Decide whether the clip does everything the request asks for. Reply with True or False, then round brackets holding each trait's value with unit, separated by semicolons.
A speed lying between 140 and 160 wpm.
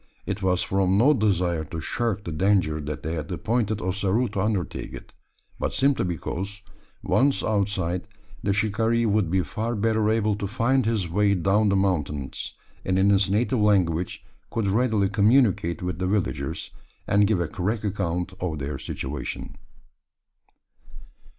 True (155 wpm)